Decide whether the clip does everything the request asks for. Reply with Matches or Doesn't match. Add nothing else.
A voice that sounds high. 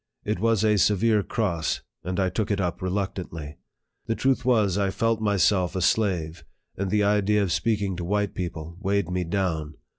Doesn't match